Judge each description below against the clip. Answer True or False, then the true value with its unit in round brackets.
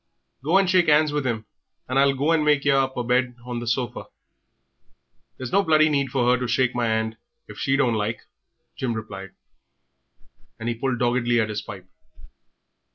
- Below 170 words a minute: False (190 wpm)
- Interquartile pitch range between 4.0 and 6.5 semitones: False (3.1 semitones)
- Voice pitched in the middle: False (125 Hz)